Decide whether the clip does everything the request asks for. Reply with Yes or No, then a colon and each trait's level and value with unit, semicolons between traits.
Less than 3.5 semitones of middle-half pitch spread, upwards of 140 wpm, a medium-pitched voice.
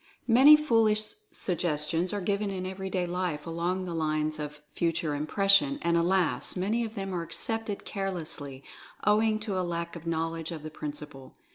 No: average, 3.8 semitones; average, 160 wpm; medium, 175 Hz